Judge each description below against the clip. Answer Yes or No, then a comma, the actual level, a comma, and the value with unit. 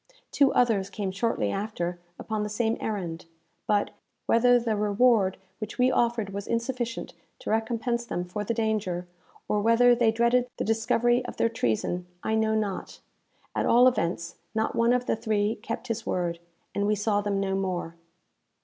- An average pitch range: Yes, average, 3.0 semitones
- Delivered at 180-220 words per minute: No, average, 170 wpm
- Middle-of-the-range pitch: No, high, 220 Hz